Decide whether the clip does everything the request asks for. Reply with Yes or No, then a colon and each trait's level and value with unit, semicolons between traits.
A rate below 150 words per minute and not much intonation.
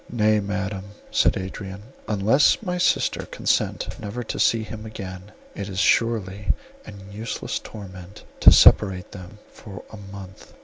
Yes: average, 140 wpm; narrow, 2.2 semitones